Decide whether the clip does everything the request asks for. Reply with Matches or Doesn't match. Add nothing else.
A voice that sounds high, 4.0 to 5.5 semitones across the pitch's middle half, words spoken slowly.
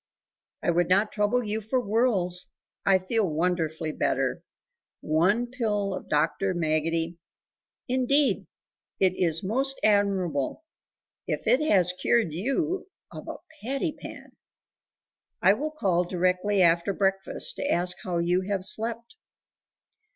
Matches